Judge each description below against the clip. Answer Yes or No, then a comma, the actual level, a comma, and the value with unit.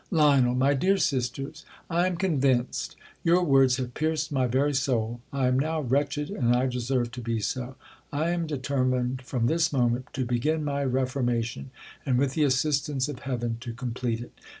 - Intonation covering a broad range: No, average, 3.0 semitones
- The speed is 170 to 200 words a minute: Yes, average, 175 wpm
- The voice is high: No, low, 130 Hz